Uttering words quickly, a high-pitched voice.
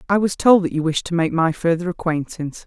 No: fast, 250 wpm; medium, 170 Hz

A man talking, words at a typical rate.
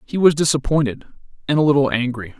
Yes: male; average, 175 wpm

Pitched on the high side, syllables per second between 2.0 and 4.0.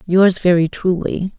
No: medium, 180 Hz; 3.9 syllables/s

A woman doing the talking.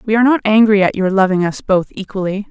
Yes: female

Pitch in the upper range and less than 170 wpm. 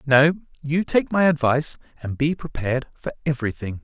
No: medium, 140 Hz; average, 155 wpm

